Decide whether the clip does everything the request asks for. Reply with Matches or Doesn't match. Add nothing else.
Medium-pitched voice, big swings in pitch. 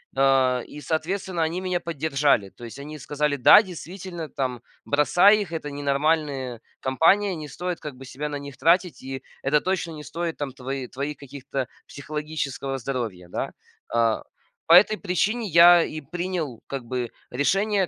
Doesn't match